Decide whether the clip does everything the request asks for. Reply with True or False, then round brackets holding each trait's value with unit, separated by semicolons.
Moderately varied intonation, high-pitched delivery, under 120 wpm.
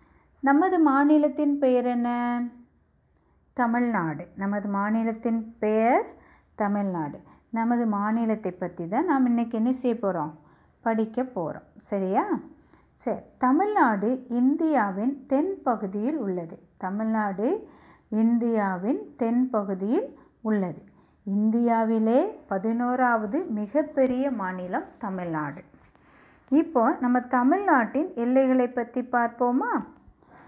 True (4.2 semitones; 235 Hz; 85 wpm)